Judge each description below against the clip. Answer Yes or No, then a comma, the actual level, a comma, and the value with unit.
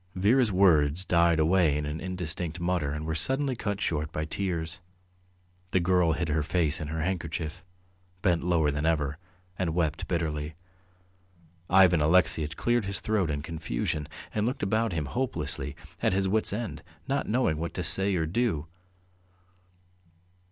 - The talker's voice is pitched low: Yes, very low, 85 Hz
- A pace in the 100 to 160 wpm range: Yes, average, 155 wpm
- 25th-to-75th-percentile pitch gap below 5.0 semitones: Yes, average, 3.6 semitones